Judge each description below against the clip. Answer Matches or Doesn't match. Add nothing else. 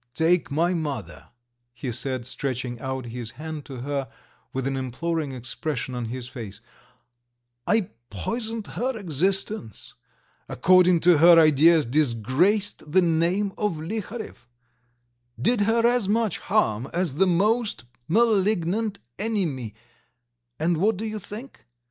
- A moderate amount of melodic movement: Doesn't match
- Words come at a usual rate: Doesn't match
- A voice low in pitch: Doesn't match